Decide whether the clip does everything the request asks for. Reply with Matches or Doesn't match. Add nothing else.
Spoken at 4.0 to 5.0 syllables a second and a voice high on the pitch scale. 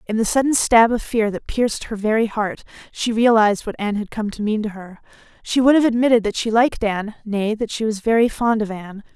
Doesn't match